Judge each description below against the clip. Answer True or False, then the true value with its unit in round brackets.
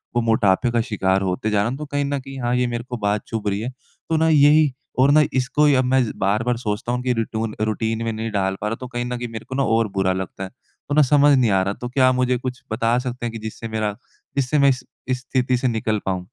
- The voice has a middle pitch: False (120 Hz)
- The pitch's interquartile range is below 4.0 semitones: True (3.1 semitones)